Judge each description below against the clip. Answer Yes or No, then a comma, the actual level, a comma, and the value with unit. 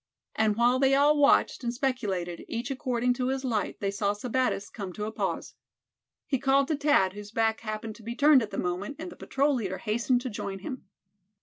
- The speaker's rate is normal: No, fast, 210 wpm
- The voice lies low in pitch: No, high, 235 Hz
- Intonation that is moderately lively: Yes, average, 4.4 semitones